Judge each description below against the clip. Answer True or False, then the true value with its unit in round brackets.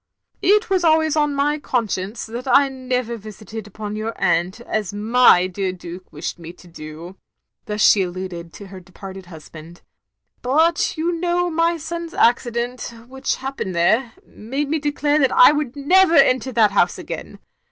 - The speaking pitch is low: False (235 Hz)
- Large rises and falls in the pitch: True (7.6 semitones)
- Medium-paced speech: True (170 wpm)